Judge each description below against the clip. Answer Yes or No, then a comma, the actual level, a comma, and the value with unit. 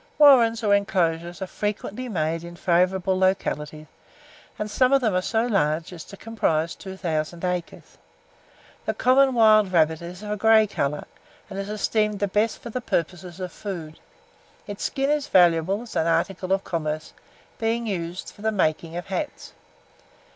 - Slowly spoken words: No, average, 165 wpm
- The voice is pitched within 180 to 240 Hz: Yes, high, 190 Hz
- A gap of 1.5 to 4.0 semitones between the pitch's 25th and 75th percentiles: No, average, 4.4 semitones